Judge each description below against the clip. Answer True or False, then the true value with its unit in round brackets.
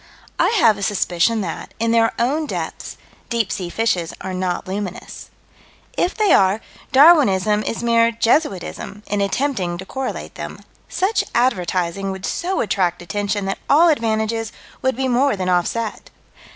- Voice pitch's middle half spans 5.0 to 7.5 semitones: False (4.6 semitones)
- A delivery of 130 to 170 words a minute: True (150 wpm)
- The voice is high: True (215 Hz)